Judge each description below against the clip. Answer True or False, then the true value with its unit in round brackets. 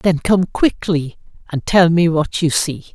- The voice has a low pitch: False (165 Hz)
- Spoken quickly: False (185 wpm)